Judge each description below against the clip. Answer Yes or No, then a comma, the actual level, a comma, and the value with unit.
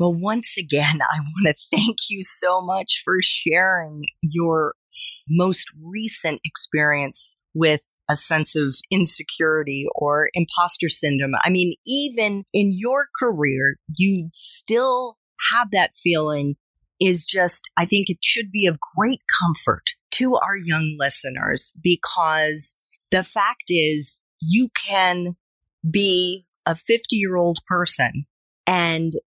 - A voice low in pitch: No, medium, 175 Hz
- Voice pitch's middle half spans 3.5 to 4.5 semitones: Yes, average, 4.2 semitones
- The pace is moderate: No, slow, 125 wpm